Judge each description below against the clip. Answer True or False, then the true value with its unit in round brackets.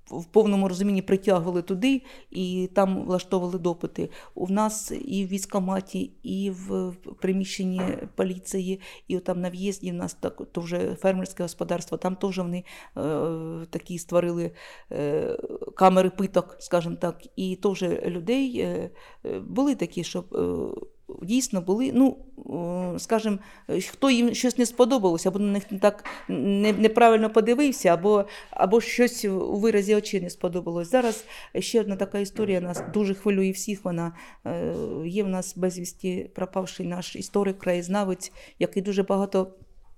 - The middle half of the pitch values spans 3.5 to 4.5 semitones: False (3.0 semitones)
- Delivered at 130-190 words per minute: True (140 wpm)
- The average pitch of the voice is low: False (195 Hz)